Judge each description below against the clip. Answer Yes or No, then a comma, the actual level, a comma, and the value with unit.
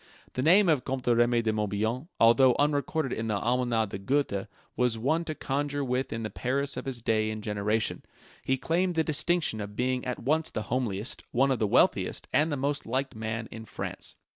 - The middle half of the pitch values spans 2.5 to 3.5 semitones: No, average, 4.3 semitones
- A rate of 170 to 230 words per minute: Yes, average, 200 wpm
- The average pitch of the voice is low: Yes, low, 125 Hz